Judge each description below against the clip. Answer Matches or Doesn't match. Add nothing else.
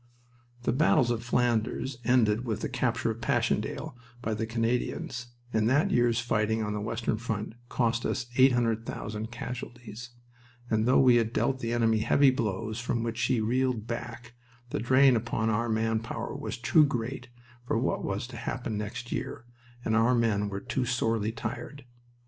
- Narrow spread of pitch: Matches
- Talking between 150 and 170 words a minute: Matches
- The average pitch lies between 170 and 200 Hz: Doesn't match